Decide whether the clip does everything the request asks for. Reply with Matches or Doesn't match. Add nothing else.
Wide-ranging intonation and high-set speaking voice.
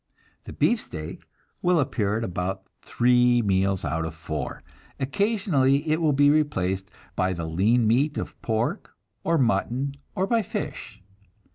Doesn't match